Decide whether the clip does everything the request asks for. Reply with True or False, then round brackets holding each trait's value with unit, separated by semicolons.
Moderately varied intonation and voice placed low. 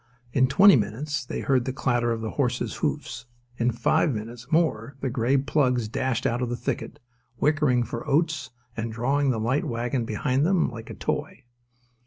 True (3.2 semitones; 125 Hz)